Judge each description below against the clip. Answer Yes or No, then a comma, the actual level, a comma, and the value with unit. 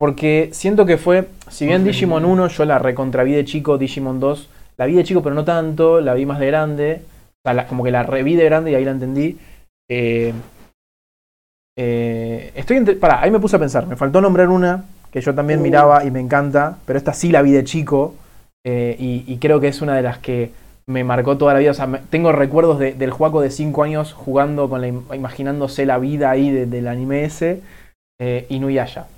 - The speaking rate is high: Yes, fast, 220 wpm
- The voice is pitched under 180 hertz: Yes, medium, 140 Hz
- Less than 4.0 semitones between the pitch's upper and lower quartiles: Yes, average, 3.5 semitones